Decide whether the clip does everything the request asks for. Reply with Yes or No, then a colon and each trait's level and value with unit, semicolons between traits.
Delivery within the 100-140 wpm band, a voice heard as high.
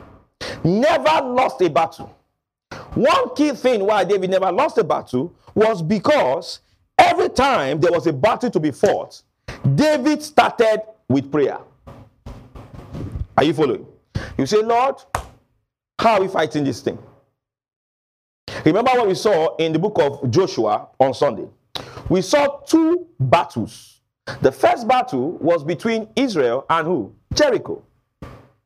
Yes: slow, 135 wpm; high, 210 Hz